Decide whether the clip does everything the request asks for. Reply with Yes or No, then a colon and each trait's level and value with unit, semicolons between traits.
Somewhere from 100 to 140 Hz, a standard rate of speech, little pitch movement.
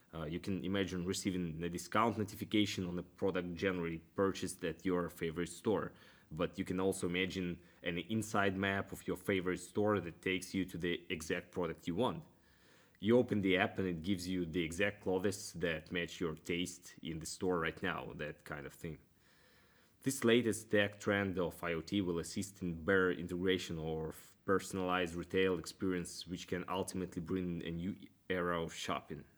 No: very low, 90 Hz; average, 175 wpm; narrow, 2.1 semitones